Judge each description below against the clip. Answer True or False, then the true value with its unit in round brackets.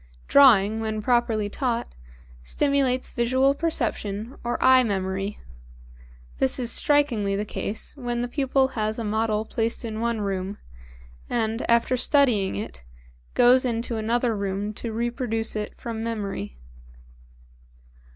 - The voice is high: True (230 Hz)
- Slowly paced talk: True (125 wpm)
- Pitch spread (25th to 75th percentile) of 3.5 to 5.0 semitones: False (3.0 semitones)